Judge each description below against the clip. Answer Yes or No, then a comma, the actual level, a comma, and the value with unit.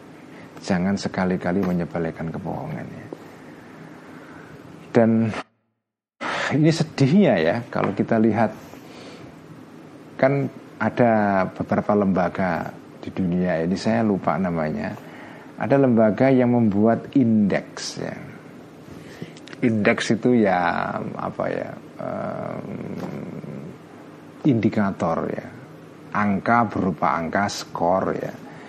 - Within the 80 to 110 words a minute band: Yes, slow, 85 wpm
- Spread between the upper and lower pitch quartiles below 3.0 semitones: No, average, 4.1 semitones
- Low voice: Yes, low, 110 Hz